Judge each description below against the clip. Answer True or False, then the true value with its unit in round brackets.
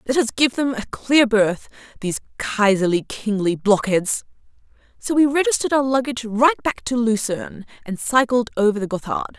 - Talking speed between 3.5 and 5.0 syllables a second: False (5.5 syllables/s)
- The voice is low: False (235 Hz)